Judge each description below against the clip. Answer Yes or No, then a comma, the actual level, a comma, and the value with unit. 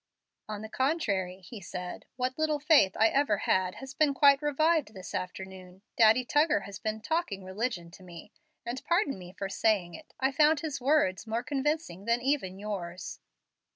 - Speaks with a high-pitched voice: Yes, high, 225 Hz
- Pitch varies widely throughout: Yes, wide, 7.2 semitones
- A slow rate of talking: No, average, 175 wpm